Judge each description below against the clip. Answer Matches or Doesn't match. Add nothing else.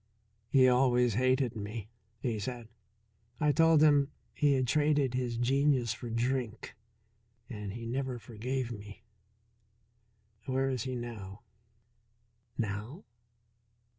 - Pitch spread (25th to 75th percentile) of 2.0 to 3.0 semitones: Matches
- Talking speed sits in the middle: Doesn't match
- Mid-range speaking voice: Doesn't match